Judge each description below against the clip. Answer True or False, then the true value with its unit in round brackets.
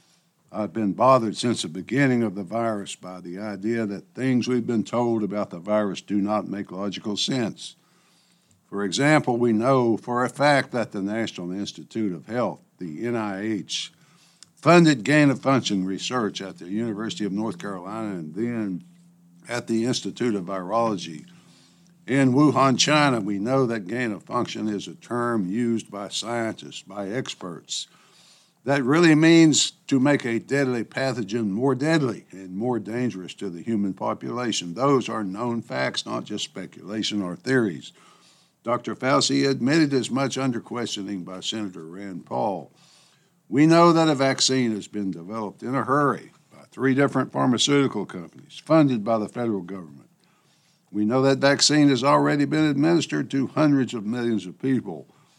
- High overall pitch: False (120 Hz)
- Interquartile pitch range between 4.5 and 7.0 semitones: True (4.9 semitones)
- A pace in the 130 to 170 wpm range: True (160 wpm)